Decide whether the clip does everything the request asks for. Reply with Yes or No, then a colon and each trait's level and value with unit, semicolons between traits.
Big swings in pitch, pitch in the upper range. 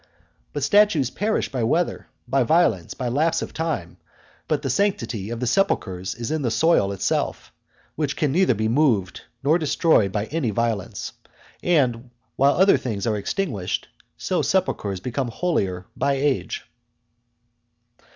No: wide, 6.4 semitones; low, 130 Hz